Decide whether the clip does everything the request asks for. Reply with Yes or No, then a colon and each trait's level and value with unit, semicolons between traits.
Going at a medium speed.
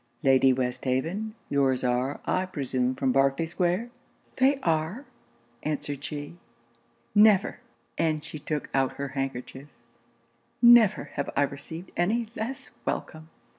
No: slow, 120 wpm